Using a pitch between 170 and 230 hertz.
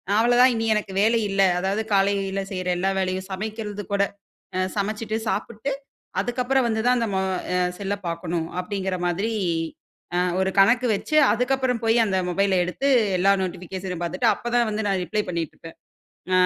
Yes: high, 200 Hz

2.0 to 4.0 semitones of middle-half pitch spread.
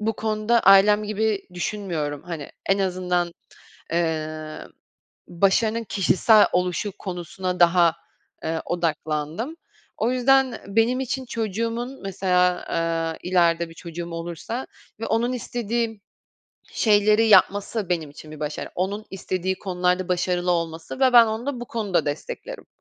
No: average, 4.6 semitones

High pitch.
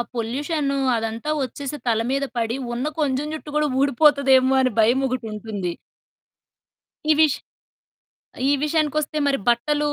Yes: very high, 270 Hz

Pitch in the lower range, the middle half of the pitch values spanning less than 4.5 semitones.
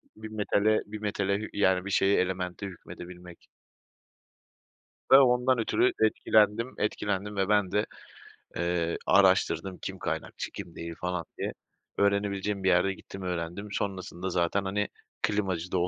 Yes: low, 100 Hz; narrow, 2.4 semitones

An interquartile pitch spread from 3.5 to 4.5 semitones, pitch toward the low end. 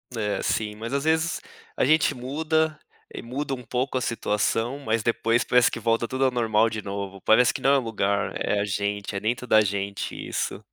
Yes: average, 4.0 semitones; low, 115 Hz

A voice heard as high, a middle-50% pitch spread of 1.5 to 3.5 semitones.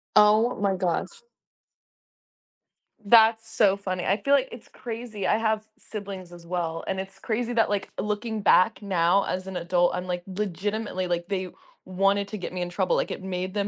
Yes: high, 195 Hz; average, 2.9 semitones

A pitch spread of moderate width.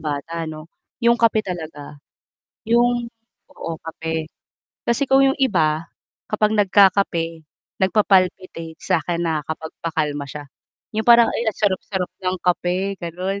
Yes: average, 4.7 semitones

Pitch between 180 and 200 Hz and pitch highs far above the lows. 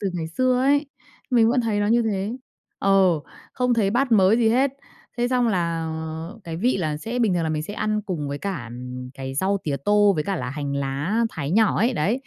Yes: high, 195 Hz; wide, 6.7 semitones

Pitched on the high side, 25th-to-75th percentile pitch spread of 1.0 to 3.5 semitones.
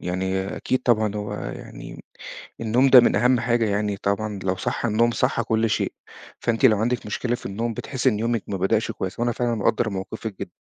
No: low, 110 Hz; average, 2.9 semitones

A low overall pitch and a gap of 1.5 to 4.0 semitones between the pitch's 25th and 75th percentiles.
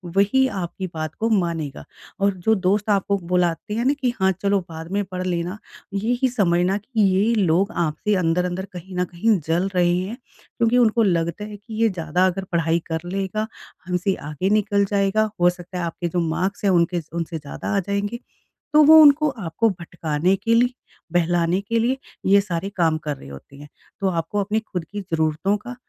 No: high, 190 Hz; average, 3.6 semitones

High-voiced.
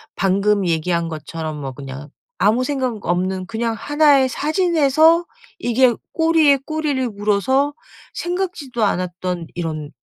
Yes: high, 225 Hz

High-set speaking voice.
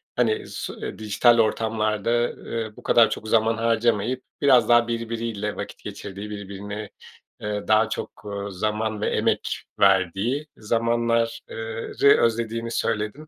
No: low, 110 Hz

